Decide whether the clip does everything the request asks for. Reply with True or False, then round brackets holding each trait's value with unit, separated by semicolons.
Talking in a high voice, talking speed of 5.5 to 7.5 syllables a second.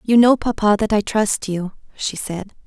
False (210 Hz; 4.5 syllables/s)